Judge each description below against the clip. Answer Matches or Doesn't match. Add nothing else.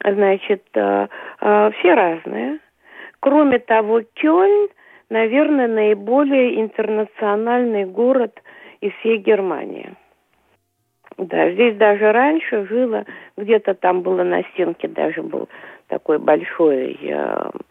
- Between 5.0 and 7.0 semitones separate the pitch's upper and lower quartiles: Doesn't match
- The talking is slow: Matches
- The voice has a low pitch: Doesn't match